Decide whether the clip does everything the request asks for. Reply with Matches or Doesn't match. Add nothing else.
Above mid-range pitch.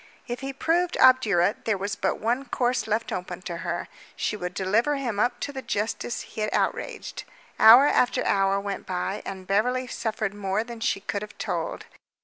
Matches